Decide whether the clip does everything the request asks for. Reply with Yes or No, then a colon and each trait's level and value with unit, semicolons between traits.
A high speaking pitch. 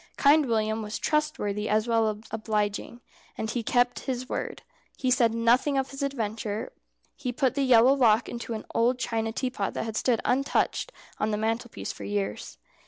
Yes: high, 230 Hz